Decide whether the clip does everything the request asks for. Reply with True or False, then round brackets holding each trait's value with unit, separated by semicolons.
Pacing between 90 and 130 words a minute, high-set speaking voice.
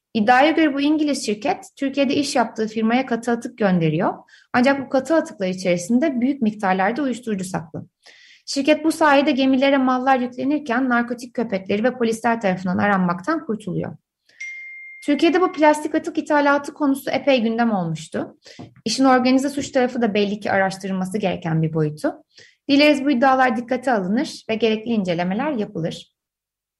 False (140 wpm; 255 Hz)